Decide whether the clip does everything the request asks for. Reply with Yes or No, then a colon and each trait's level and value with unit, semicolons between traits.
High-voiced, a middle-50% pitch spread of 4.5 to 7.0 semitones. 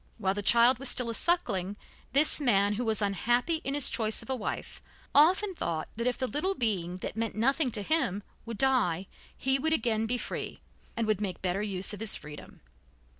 Yes: high, 230 Hz; average, 4.8 semitones